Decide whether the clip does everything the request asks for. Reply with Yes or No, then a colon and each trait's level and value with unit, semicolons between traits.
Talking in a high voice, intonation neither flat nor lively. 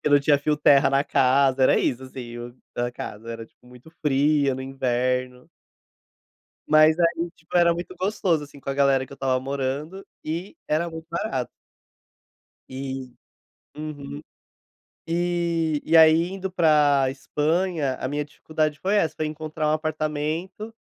No: medium, 150 Hz; average, 3.6 semitones